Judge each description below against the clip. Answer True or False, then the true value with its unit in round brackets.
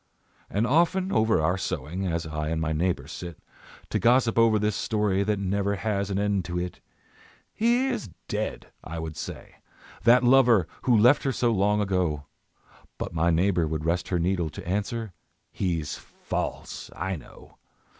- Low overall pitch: True (95 Hz)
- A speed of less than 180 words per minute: True (165 wpm)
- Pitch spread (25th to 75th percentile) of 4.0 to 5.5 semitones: True (4.9 semitones)